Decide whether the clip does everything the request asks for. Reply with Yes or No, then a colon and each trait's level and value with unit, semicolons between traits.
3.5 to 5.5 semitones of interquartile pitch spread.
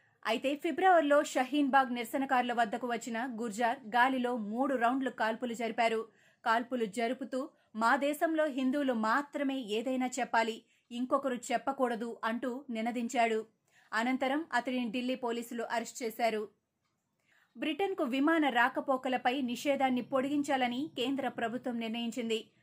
No: narrow, 2.6 semitones